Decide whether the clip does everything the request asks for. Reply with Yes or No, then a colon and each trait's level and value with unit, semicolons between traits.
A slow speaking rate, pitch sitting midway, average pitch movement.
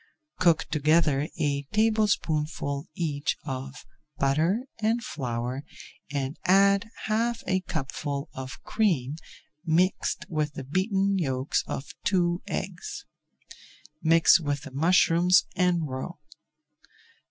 Yes: slow, 105 wpm; medium, 160 Hz; average, 4.9 semitones